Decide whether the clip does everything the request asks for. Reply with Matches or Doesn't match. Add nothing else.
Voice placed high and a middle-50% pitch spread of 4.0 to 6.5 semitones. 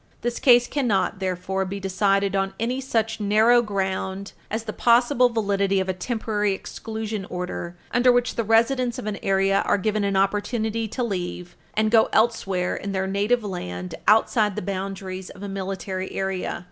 Doesn't match